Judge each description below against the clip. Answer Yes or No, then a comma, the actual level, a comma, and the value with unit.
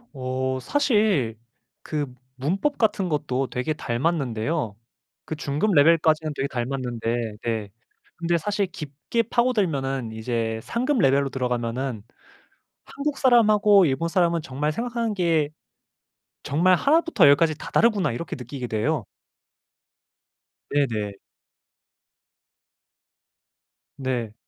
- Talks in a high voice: No, medium, 145 Hz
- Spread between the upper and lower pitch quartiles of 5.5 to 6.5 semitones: No, wide, 7.3 semitones